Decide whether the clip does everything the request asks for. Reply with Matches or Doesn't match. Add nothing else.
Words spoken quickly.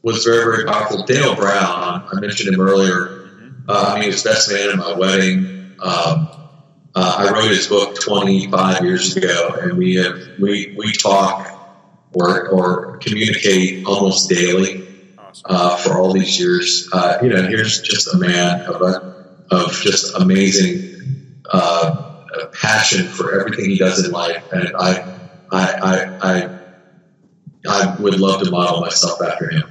Doesn't match